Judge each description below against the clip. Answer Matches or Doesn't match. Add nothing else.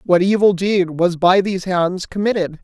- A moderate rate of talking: Matches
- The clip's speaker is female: Doesn't match